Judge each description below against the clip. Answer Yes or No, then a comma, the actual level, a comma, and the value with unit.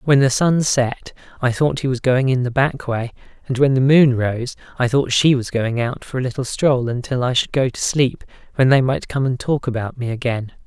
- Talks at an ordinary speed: No, fast, 240 wpm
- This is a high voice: No, low, 130 Hz